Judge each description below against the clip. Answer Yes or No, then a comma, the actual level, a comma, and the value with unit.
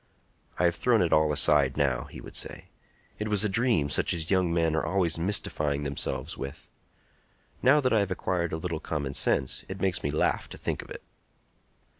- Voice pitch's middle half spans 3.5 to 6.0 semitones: Yes, average, 4.7 semitones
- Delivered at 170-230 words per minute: Yes, average, 200 wpm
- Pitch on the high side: No, very low, 85 Hz